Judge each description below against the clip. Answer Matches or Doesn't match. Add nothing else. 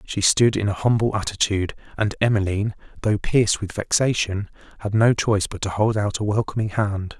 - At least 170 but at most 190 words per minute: Matches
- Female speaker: Doesn't match